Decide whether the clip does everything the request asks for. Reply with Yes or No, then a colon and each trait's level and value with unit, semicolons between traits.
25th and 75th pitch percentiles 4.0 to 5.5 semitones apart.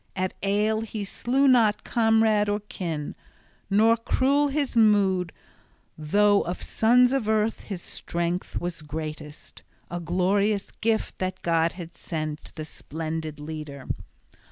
Yes: average, 5.1 semitones